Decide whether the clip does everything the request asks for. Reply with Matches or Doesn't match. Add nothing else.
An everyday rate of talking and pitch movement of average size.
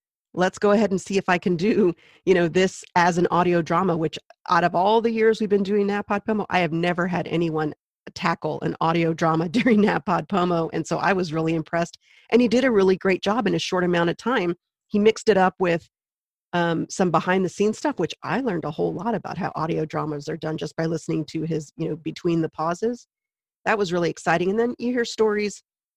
Doesn't match